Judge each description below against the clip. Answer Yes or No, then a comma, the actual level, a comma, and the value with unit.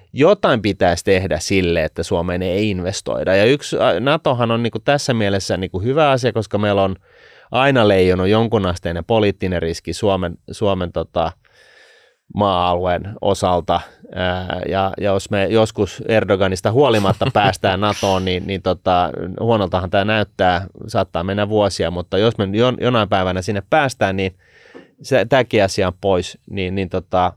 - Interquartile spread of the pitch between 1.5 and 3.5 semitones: Yes, average, 2.8 semitones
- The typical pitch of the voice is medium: No, very low, 95 Hz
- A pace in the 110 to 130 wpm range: No, average, 145 wpm